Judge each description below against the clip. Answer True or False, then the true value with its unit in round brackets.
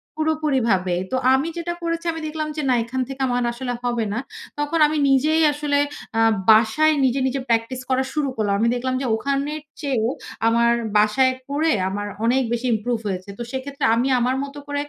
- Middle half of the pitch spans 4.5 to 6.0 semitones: False (4.0 semitones)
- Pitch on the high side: True (260 Hz)